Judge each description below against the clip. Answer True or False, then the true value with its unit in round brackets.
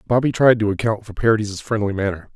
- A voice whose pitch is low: True (105 Hz)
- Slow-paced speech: False (205 wpm)